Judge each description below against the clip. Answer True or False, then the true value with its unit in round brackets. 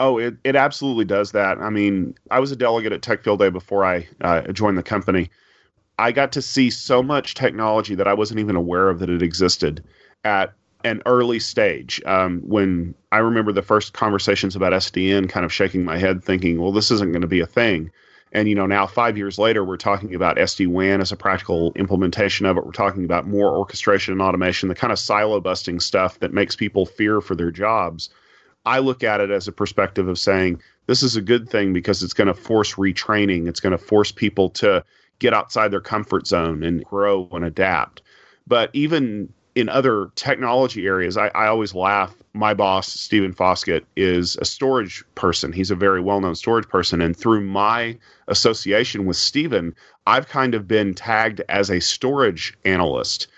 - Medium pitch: False (100 Hz)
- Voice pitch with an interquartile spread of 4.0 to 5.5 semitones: False (2.9 semitones)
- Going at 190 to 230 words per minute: True (200 wpm)